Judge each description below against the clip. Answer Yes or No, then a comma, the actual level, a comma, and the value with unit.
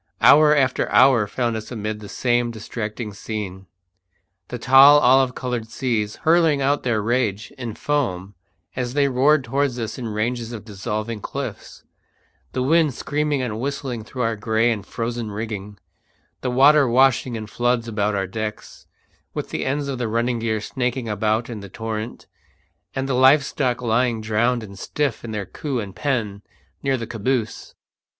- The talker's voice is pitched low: Yes, low, 120 Hz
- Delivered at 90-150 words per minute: No, average, 165 wpm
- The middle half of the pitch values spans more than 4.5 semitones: No, average, 3.4 semitones